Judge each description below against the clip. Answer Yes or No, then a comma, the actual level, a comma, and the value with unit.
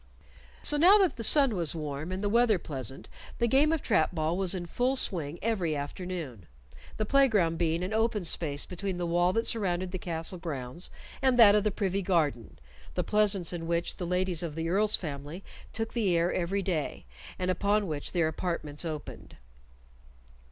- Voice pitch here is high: No, medium, 180 Hz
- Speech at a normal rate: Yes, average, 185 wpm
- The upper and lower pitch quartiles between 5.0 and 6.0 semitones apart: No, average, 4.3 semitones